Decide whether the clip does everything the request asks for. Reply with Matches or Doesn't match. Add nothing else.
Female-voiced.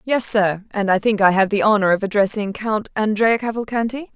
Matches